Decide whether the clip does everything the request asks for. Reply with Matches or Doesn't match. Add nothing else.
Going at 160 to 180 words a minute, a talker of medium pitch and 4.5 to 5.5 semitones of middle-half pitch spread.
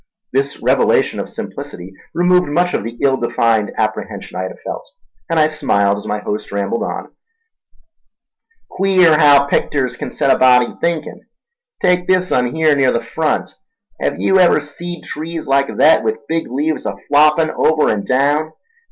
Matches